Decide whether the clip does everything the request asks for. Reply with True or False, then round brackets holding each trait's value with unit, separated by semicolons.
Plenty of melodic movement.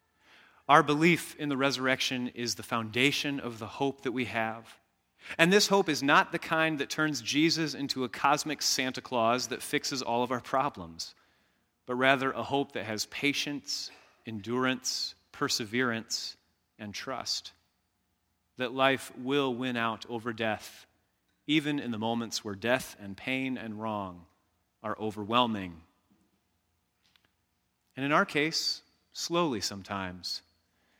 False (4.6 semitones)